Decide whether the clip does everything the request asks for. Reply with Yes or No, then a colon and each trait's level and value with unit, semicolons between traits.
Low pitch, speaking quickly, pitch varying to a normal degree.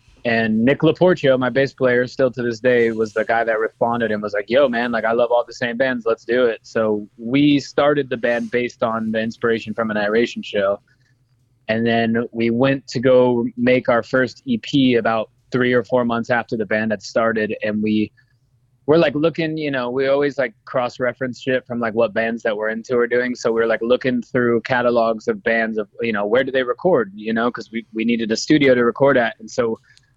No: low, 120 Hz; fast, 225 wpm; narrow, 2.1 semitones